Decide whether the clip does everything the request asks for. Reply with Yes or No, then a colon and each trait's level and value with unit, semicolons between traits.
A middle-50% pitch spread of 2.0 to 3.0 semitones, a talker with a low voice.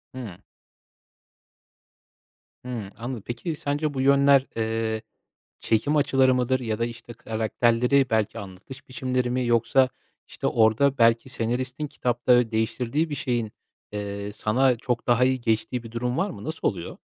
Yes: average, 2.7 semitones; low, 120 Hz